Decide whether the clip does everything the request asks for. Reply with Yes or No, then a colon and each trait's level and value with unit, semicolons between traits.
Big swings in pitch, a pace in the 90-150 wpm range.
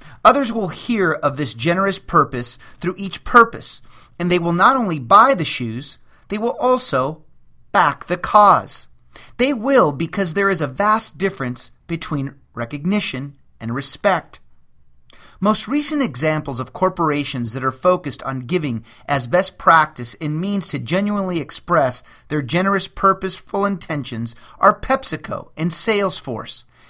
Yes: wide, 6.9 semitones; average, 140 wpm